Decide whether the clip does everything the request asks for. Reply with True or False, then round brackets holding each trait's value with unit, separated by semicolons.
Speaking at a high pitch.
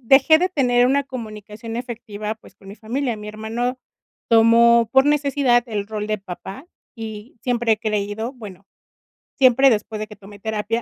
True (225 Hz)